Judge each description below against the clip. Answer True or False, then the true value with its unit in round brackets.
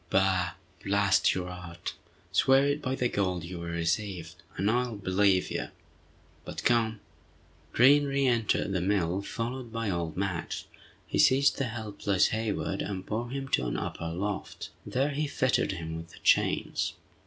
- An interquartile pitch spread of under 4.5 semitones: False (5.0 semitones)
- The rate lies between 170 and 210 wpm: False (155 wpm)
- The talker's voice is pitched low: True (100 Hz)